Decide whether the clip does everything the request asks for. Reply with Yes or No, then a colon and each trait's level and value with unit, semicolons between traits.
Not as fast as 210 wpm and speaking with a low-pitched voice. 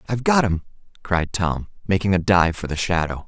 Yes: average, 200 wpm; very low, 95 Hz